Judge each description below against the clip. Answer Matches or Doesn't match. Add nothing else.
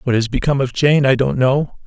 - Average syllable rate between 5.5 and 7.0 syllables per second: Matches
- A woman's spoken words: Doesn't match